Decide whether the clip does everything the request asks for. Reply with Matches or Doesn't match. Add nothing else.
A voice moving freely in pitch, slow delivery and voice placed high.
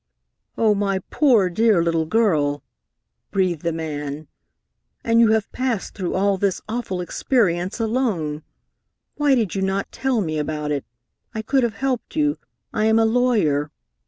Doesn't match